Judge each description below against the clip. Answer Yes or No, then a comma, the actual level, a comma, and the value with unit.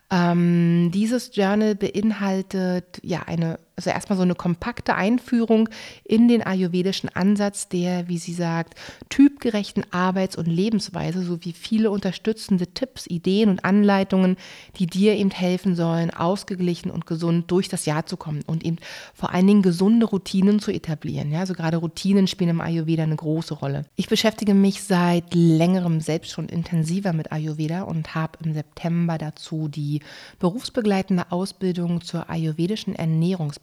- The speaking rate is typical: Yes, average, 150 wpm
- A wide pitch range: No, average, 2.9 semitones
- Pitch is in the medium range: Yes, medium, 180 Hz